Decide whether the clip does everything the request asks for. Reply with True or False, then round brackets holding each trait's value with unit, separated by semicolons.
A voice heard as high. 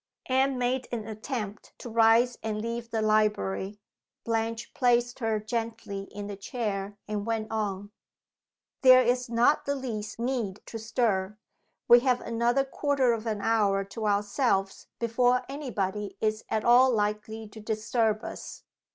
True (225 Hz)